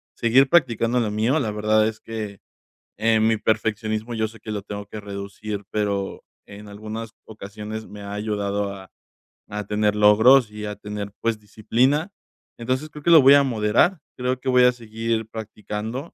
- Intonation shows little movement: Yes, narrow, 2.1 semitones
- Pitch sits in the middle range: No, low, 110 Hz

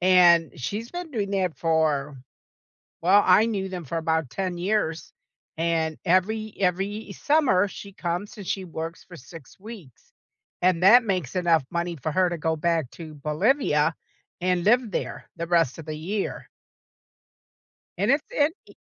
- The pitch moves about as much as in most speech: Yes, average, 3.8 semitones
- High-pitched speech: No, medium, 180 Hz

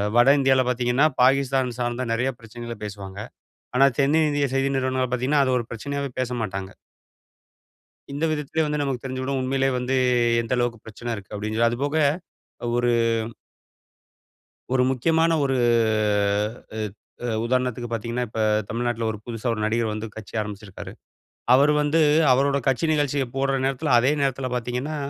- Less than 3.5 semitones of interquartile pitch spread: Yes, average, 2.7 semitones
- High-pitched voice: No, low, 125 Hz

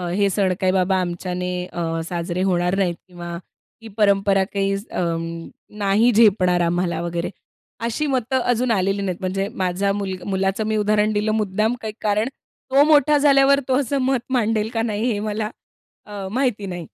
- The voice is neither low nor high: No, high, 200 Hz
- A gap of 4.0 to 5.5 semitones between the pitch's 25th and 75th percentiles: No, average, 3.3 semitones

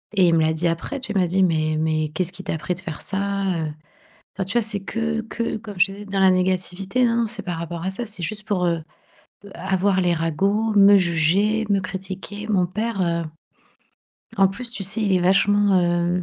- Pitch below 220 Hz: Yes, high, 190 Hz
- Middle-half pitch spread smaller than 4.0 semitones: Yes, average, 2.9 semitones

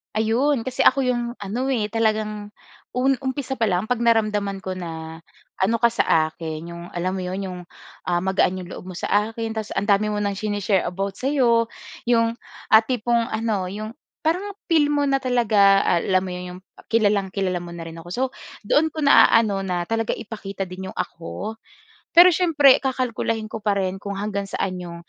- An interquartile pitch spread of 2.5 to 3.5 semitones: No, average, 4.0 semitones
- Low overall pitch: No, high, 210 Hz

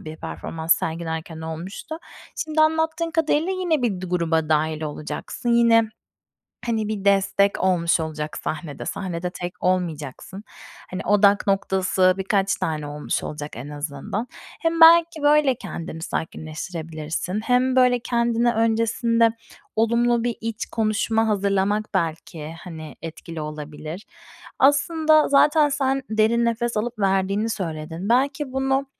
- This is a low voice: No, high, 200 Hz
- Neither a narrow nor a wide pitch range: No, wide, 6.9 semitones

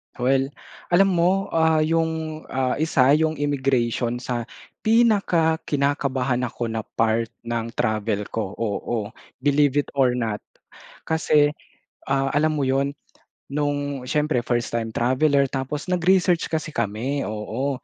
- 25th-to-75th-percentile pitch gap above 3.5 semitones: Yes, average, 4.5 semitones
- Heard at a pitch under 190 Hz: Yes, medium, 140 Hz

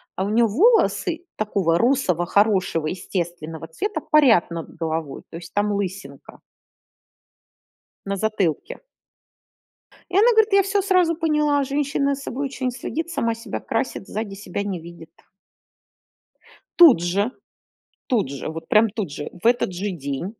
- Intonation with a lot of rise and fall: Yes, wide, 8.3 semitones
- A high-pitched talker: Yes, high, 210 Hz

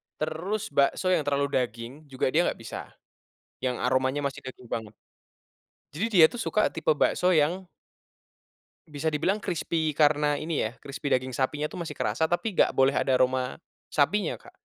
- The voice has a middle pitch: Yes, medium, 150 Hz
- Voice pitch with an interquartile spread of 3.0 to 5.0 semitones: Yes, average, 4.0 semitones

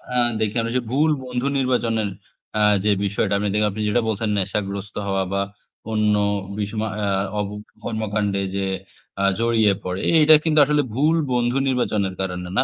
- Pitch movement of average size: Yes, average, 3.8 semitones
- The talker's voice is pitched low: Yes, low, 110 Hz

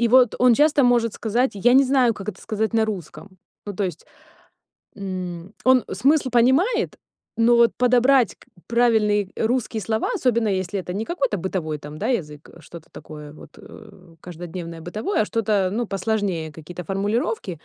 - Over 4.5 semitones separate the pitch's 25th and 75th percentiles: Yes, average, 5.0 semitones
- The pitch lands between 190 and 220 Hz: Yes, high, 215 Hz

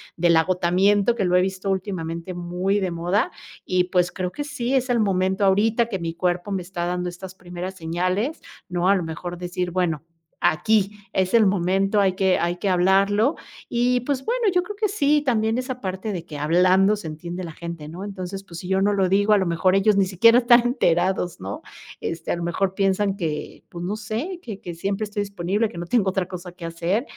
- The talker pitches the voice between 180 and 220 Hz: Yes, high, 190 Hz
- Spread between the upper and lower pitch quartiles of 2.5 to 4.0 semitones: Yes, average, 2.9 semitones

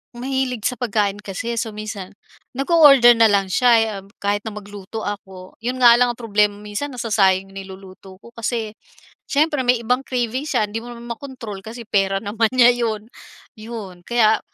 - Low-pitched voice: No, high, 225 Hz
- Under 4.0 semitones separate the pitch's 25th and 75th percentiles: Yes, average, 3.1 semitones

